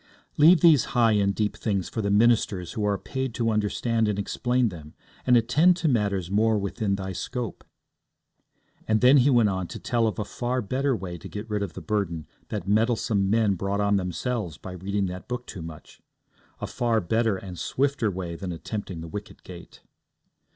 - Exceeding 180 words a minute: Yes, average, 195 wpm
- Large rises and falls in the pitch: No, average, 3.9 semitones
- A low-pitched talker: Yes, low, 105 Hz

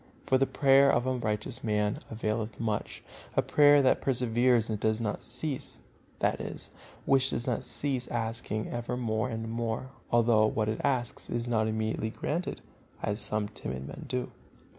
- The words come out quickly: No, average, 165 wpm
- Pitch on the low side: Yes, low, 115 Hz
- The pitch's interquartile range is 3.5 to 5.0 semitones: No, average, 2.7 semitones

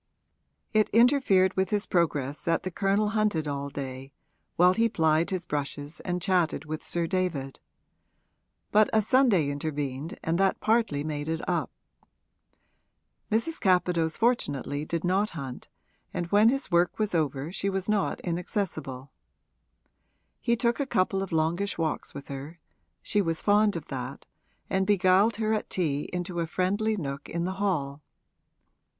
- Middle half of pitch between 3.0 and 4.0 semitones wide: No, average, 5.2 semitones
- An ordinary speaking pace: Yes, average, 150 wpm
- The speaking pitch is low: No, medium, 175 Hz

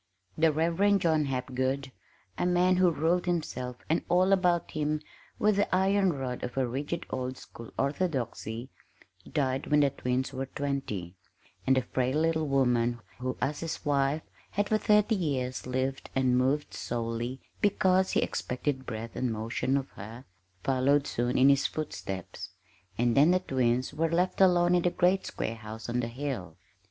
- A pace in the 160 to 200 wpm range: Yes, average, 165 wpm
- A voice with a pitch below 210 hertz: Yes, medium, 140 Hz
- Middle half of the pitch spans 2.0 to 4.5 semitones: No, average, 5.2 semitones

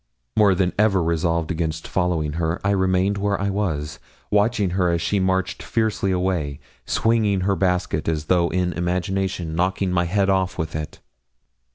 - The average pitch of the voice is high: No, very low, 90 Hz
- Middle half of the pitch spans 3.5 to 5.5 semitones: No, average, 2.7 semitones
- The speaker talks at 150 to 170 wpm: Yes, average, 165 wpm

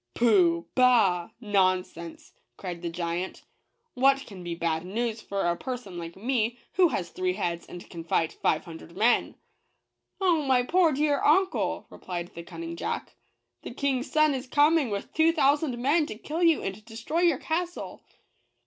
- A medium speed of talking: Yes, average, 180 wpm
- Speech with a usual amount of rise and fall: No, wide, 8.6 semitones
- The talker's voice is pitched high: Yes, high, 230 Hz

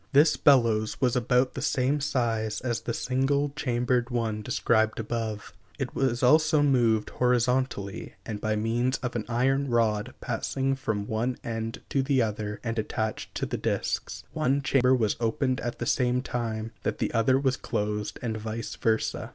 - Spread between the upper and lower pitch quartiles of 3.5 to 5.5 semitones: No, average, 2.9 semitones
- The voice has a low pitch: Yes, low, 120 Hz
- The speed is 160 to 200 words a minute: Yes, average, 170 wpm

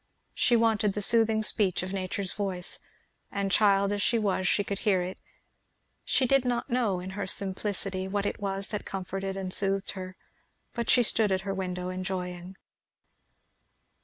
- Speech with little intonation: Yes, narrow, 2.0 semitones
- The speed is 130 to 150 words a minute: No, average, 165 wpm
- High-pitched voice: Yes, high, 195 Hz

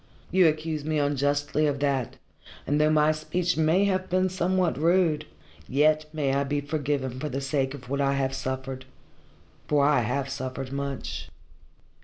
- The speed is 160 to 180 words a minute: Yes, average, 165 wpm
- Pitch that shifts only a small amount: Yes, narrow, 2.3 semitones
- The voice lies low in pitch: No, medium, 145 Hz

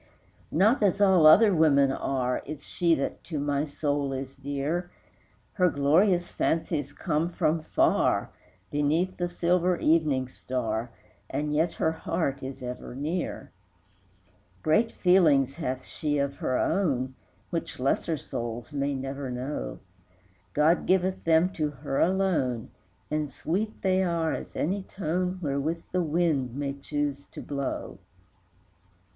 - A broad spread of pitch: No, average, 4.1 semitones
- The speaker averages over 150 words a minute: No, slow, 135 wpm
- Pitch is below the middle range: No, medium, 150 Hz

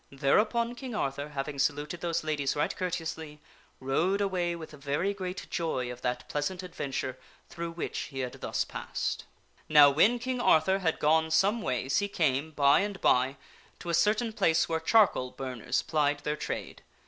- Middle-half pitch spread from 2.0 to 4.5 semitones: No, average, 5.1 semitones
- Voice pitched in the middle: Yes, medium, 160 Hz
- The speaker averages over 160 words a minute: Yes, average, 170 wpm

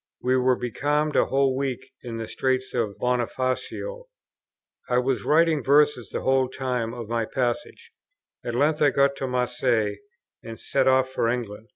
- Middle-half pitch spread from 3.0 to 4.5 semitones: No, narrow, 2.4 semitones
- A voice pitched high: No, low, 130 Hz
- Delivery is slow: No, average, 165 wpm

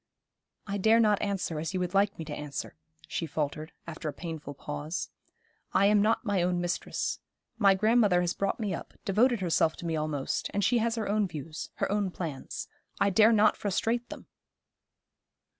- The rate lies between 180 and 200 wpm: Yes, average, 185 wpm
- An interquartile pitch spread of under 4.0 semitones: No, average, 4.5 semitones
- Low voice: No, high, 190 Hz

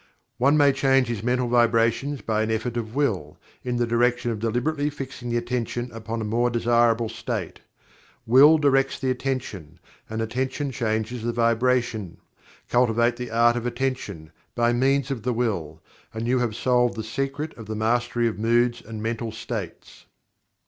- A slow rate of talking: No, average, 165 wpm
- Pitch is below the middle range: Yes, low, 120 Hz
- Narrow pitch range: Yes, narrow, 2.1 semitones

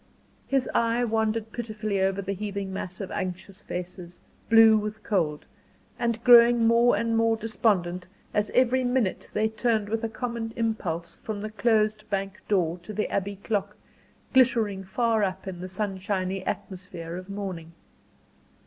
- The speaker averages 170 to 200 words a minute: No, average, 150 wpm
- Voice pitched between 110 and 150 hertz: No, high, 210 Hz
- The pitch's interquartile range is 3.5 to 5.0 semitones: No, average, 3.1 semitones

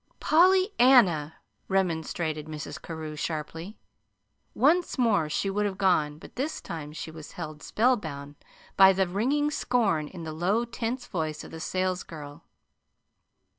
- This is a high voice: No, medium, 180 Hz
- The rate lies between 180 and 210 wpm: No, slow, 135 wpm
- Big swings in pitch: Yes, wide, 6.8 semitones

